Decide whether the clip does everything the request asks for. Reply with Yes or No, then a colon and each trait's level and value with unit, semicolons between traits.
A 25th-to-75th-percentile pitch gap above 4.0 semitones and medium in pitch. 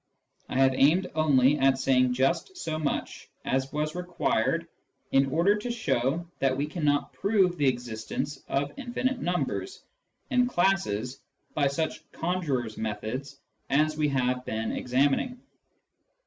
Yes: average, 5.0 semitones; medium, 145 Hz